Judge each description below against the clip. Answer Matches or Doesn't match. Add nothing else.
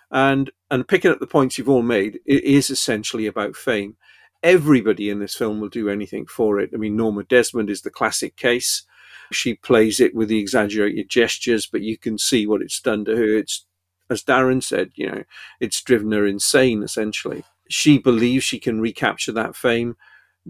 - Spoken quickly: Doesn't match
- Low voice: Matches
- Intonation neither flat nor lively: Matches